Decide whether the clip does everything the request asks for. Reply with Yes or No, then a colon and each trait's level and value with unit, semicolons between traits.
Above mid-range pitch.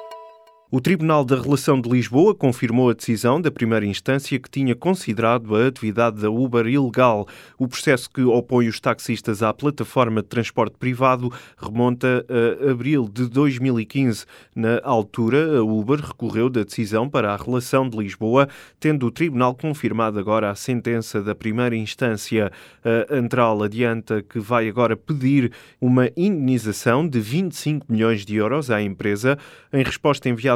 No: low, 120 Hz